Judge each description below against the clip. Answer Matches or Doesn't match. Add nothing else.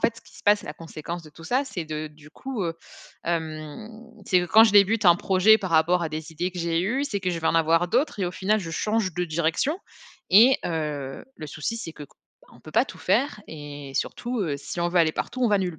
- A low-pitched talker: Doesn't match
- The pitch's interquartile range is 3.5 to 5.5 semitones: Matches